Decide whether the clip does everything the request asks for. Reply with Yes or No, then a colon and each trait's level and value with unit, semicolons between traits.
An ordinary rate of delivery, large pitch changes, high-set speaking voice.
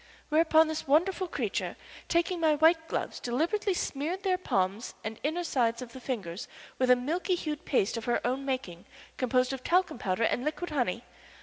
Yes: average, 180 wpm; wide, 5.7 semitones; very high, 275 Hz